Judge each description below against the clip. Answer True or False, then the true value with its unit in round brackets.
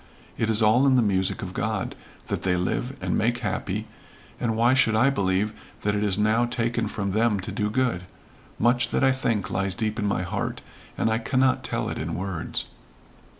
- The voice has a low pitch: True (110 Hz)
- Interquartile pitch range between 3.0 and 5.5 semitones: True (3.3 semitones)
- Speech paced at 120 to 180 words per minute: False (200 wpm)